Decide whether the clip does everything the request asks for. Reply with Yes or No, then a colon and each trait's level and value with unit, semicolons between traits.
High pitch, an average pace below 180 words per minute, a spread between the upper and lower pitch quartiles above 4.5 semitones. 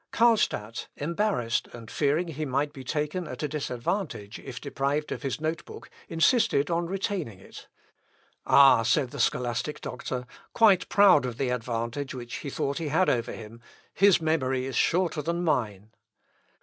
No: medium, 140 Hz; average, 160 wpm; average, 5.3 semitones